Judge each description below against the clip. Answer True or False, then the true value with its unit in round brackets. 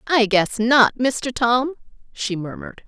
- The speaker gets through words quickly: False (145 wpm)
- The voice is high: True (240 Hz)